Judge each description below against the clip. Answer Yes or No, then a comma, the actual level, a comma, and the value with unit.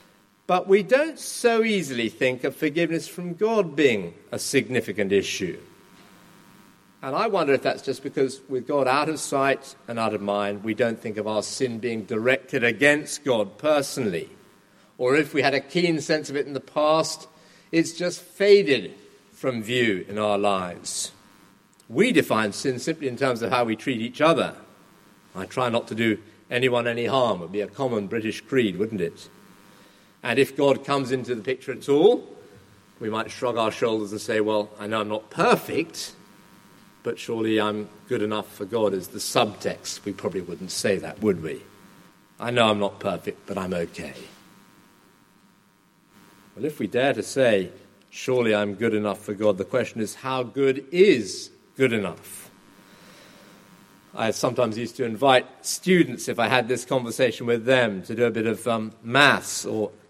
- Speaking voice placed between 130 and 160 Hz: No, low, 120 Hz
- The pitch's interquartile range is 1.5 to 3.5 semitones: No, average, 5.0 semitones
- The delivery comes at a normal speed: Yes, average, 180 wpm